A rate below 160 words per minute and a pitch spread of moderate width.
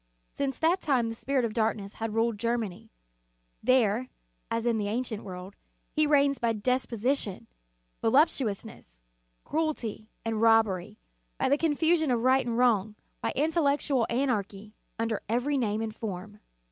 Yes: average, 150 wpm; average, 4.0 semitones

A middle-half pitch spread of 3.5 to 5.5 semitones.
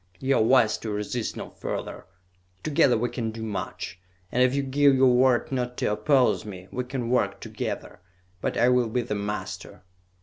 No: average, 3.1 semitones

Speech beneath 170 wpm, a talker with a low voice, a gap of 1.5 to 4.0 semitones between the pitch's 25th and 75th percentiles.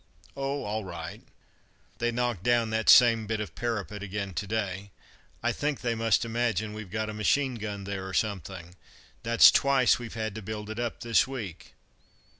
No: average, 180 wpm; low, 110 Hz; average, 2.7 semitones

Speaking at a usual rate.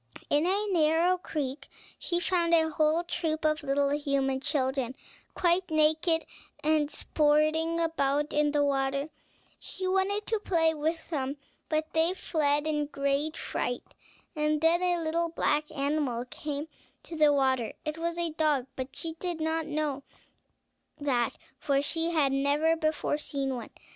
Yes: average, 155 wpm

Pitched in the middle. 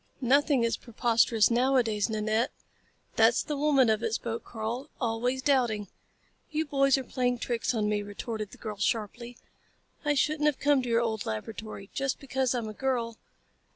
No: high, 235 Hz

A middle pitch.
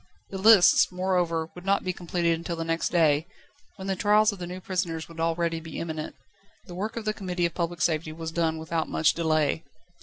Yes: medium, 170 Hz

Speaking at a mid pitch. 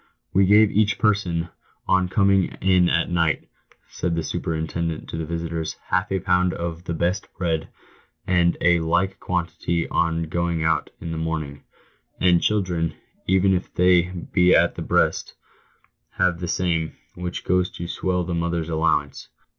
No: very low, 85 Hz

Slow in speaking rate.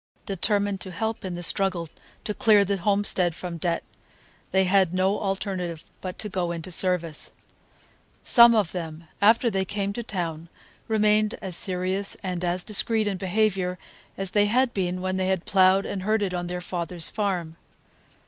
No: average, 165 wpm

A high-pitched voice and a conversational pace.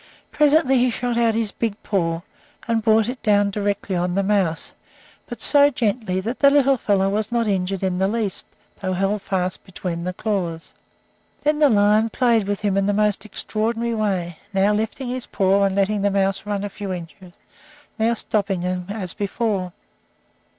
Yes: high, 205 Hz; average, 180 wpm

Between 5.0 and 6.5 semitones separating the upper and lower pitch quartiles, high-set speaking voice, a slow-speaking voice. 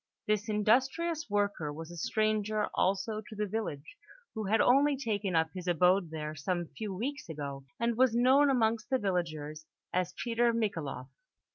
No: wide, 5.4 semitones; high, 210 Hz; average, 160 wpm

